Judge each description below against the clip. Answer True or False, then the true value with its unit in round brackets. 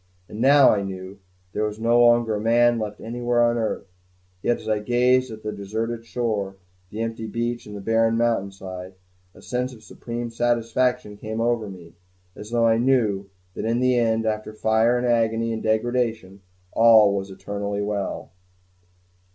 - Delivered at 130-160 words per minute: False (170 wpm)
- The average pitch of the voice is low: True (115 Hz)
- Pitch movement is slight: True (2.3 semitones)